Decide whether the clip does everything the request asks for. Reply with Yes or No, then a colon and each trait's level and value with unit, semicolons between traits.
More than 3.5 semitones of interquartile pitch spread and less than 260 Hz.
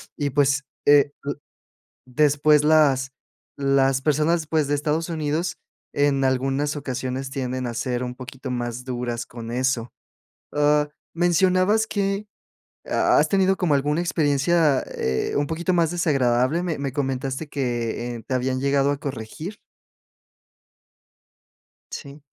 No: average, 3.2 semitones; medium, 140 Hz